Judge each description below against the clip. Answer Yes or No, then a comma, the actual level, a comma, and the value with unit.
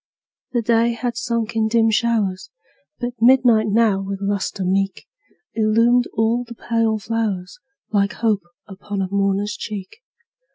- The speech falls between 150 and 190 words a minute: No, slow, 135 wpm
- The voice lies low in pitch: No, high, 220 Hz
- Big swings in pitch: No, average, 2.8 semitones